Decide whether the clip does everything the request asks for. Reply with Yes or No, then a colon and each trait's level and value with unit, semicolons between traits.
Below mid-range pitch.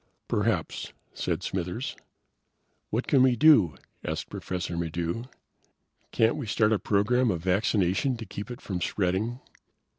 Yes: low, 105 Hz